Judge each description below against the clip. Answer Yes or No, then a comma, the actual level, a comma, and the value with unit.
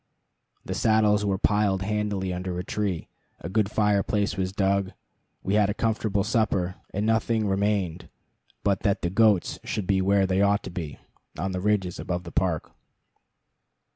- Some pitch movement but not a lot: No, narrow, 2.1 semitones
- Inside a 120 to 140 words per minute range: No, average, 165 wpm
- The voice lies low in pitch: Yes, low, 100 Hz